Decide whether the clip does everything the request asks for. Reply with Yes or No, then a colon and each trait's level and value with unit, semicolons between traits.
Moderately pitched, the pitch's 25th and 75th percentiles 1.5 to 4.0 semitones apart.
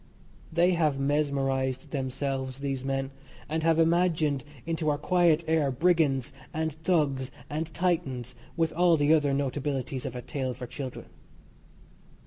Yes: medium, 145 Hz; average, 3.2 semitones